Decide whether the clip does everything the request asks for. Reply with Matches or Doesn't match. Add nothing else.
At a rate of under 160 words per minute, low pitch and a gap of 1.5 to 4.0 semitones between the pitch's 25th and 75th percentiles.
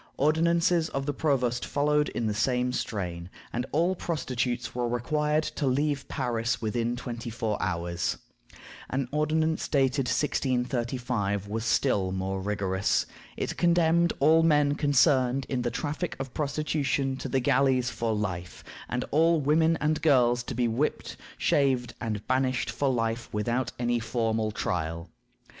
Doesn't match